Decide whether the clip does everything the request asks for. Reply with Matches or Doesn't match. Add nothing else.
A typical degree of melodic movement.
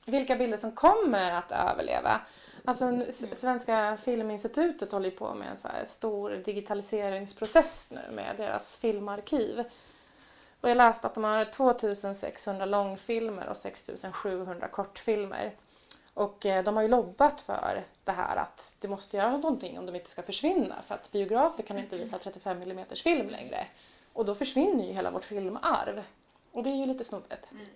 Matches